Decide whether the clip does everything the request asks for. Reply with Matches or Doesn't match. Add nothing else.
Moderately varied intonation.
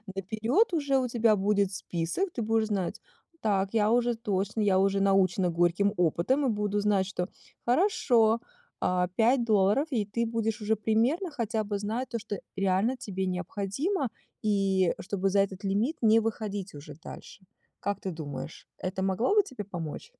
Matches